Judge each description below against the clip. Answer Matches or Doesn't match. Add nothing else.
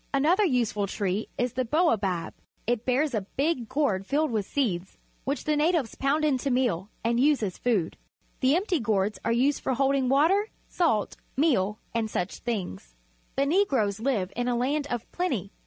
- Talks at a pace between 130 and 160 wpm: Doesn't match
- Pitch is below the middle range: Doesn't match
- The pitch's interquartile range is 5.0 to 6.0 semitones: Matches